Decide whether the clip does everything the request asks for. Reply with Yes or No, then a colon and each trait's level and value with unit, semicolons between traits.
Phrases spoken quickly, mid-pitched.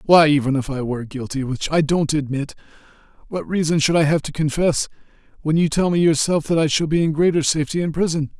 Yes: fast, 220 wpm; medium, 155 Hz